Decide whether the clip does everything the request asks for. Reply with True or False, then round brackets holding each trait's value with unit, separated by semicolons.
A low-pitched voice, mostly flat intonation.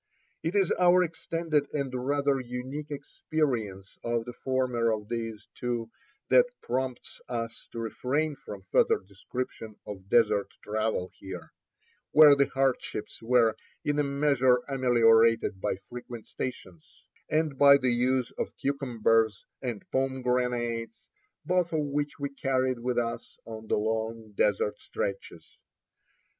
False (125 Hz; 3.7 semitones)